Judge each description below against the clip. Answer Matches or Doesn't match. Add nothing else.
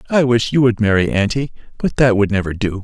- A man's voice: Matches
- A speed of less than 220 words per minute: Doesn't match